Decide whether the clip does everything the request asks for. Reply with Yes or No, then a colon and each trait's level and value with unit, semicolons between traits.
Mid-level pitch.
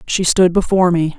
Yes: medium, 175 Hz